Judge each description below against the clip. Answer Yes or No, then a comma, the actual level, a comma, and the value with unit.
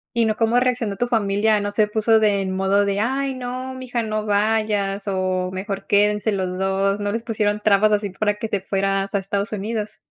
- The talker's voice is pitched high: Yes, high, 210 Hz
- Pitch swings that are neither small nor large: No, narrow, 2.1 semitones